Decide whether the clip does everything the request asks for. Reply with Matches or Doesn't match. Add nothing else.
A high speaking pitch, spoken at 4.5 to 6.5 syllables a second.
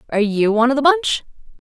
Doesn't match